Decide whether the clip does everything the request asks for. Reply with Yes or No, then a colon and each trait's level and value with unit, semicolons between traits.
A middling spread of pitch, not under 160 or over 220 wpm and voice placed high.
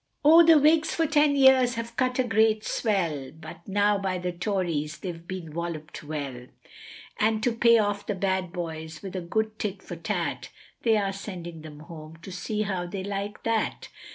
Yes: average, 4.7 semitones; average, 185 wpm; high, 195 Hz